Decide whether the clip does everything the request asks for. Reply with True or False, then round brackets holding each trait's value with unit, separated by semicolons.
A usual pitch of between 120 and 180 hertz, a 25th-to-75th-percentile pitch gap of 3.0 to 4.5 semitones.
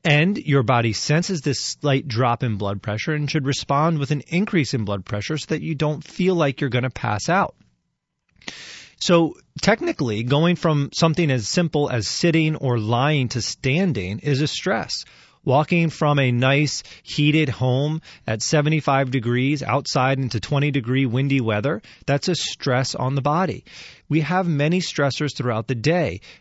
True (140 Hz; 3.9 semitones)